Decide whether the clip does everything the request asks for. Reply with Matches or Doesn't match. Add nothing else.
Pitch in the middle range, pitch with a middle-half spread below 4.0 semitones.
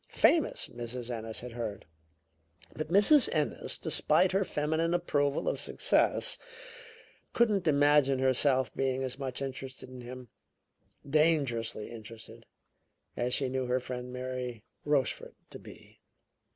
Doesn't match